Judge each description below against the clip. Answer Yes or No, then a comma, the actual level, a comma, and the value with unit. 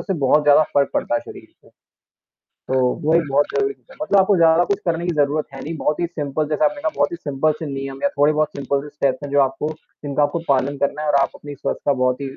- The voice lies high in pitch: No, medium, 145 Hz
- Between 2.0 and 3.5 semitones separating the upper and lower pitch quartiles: Yes, average, 2.8 semitones